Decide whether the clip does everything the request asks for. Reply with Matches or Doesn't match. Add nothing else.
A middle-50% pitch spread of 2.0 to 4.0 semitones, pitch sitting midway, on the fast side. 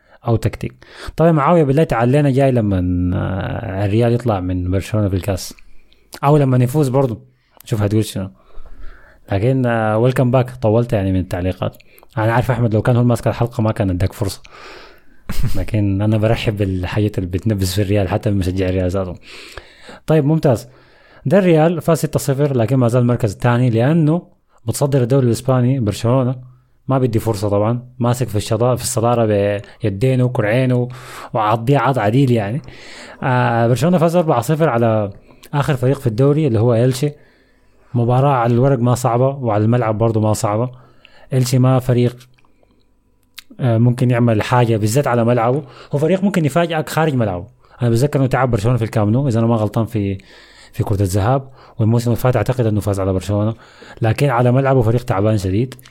Doesn't match